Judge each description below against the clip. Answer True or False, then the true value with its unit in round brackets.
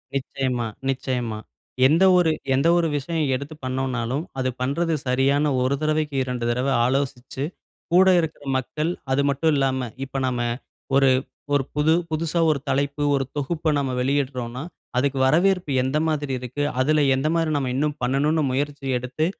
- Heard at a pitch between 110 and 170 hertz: True (140 Hz)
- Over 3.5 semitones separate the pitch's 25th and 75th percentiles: False (2.9 semitones)